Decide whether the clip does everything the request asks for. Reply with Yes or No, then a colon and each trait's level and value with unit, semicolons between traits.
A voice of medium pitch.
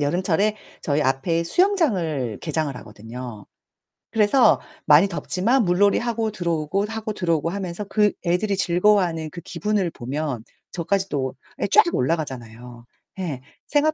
Yes: medium, 170 Hz